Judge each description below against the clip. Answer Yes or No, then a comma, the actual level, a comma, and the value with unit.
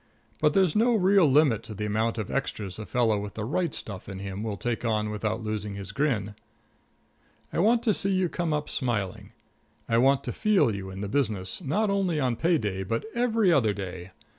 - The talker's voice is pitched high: No, low, 115 Hz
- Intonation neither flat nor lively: No, wide, 8.5 semitones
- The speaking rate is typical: No, fast, 210 wpm